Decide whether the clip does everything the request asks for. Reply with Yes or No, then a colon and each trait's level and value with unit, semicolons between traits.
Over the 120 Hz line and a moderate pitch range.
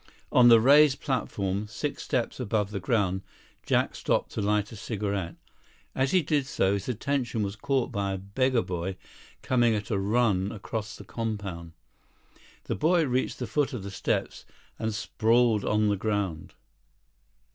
No: low, 105 Hz; average, 3.8 semitones